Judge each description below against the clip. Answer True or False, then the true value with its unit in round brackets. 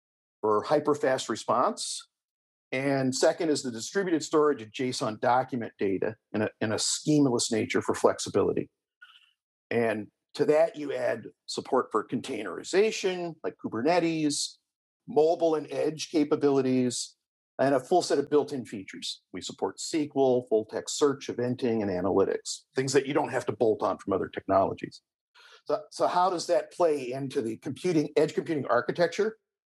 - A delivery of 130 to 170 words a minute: True (150 wpm)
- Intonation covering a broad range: True (5.8 semitones)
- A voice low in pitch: False (150 Hz)